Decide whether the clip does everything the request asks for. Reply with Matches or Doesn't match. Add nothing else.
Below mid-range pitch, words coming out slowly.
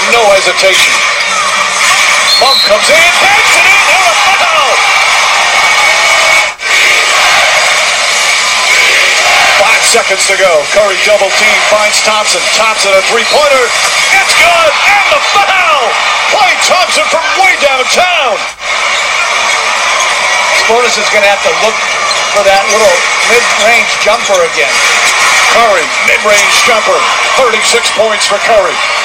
Doesn't match